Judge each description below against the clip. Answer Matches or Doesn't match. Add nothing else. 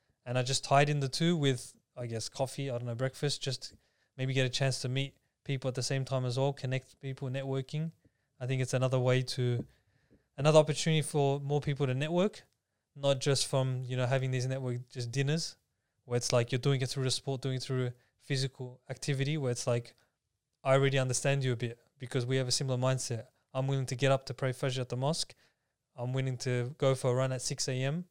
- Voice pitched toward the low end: Matches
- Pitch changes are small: Matches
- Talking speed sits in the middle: Doesn't match